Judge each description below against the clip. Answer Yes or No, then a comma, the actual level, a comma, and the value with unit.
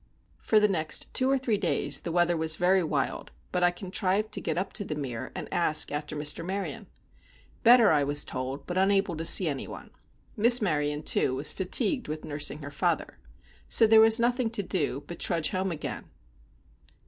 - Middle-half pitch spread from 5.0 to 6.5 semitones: Yes, wide, 5.4 semitones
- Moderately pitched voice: Yes, medium, 175 Hz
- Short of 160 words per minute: No, average, 195 wpm